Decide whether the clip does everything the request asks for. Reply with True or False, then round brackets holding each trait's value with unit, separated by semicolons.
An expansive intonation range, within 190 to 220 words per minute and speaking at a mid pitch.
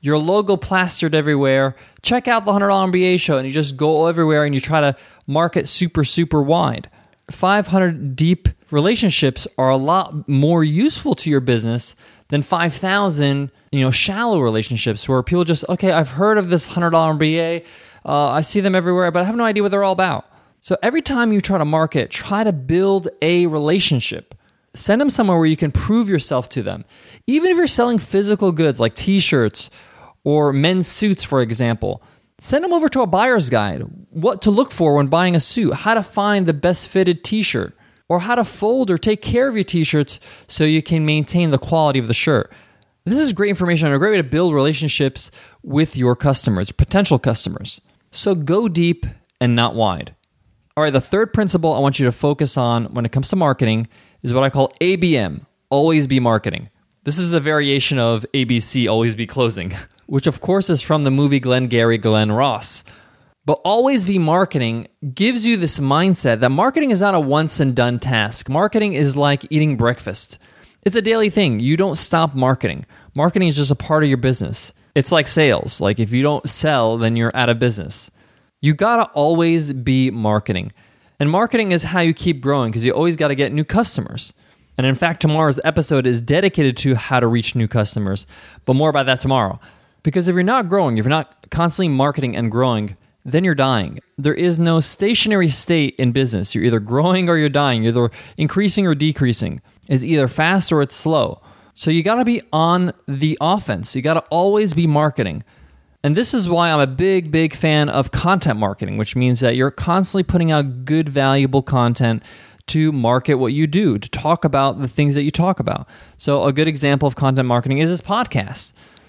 True (5.7 semitones; 200 wpm; 150 Hz)